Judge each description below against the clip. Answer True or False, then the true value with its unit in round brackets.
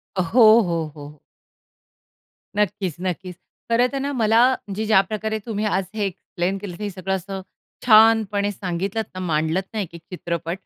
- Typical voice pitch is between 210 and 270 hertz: False (195 Hz)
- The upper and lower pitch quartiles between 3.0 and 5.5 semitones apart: True (3.6 semitones)